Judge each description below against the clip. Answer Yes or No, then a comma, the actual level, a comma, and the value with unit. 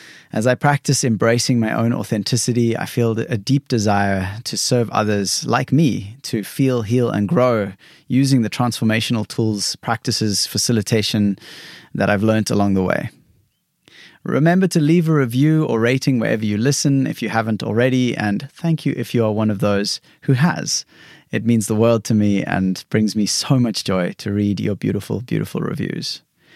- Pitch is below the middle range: Yes, low, 115 Hz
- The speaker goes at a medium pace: Yes, average, 175 wpm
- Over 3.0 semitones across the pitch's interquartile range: Yes, average, 4.1 semitones